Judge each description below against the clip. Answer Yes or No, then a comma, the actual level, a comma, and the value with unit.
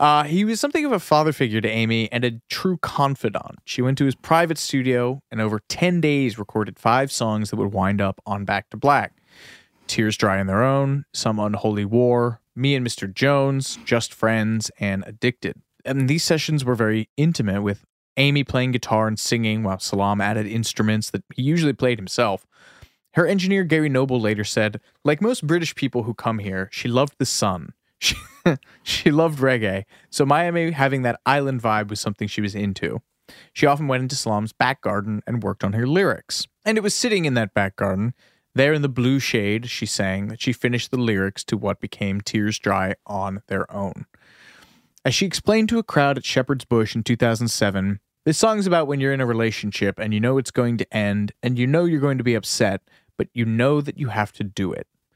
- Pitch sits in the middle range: No, low, 120 Hz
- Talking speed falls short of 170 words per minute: No, fast, 205 wpm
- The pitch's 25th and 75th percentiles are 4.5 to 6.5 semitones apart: Yes, average, 4.9 semitones